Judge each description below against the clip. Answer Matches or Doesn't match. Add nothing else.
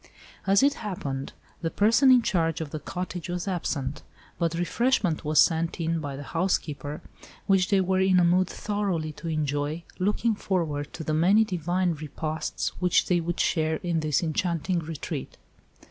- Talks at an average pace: Matches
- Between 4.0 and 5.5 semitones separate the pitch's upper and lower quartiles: Doesn't match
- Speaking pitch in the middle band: Matches